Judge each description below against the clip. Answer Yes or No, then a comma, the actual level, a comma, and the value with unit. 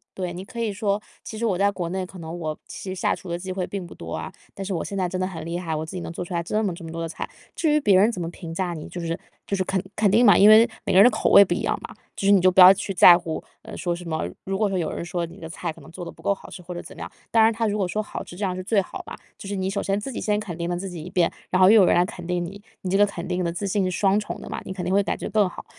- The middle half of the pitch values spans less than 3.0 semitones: Yes, narrow, 2.5 semitones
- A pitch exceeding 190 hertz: No, medium, 185 Hz